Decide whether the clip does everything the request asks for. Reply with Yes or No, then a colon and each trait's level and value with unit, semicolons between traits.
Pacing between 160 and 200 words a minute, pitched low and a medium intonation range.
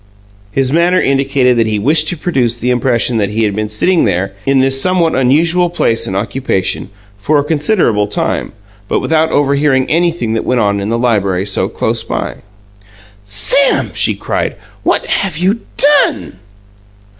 No: average, 165 wpm; low, 130 Hz; wide, 6.9 semitones